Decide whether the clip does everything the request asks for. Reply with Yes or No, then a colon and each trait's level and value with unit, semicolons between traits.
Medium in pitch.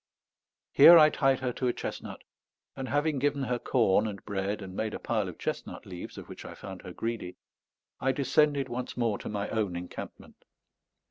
No: low, 120 Hz